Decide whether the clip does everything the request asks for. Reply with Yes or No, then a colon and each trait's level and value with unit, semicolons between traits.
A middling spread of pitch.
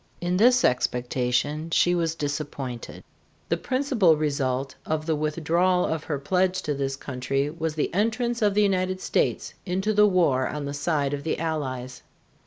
Yes: average, 4.7 semitones